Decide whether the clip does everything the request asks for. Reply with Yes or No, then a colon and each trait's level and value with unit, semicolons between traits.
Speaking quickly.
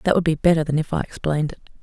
Yes: fast, 295 wpm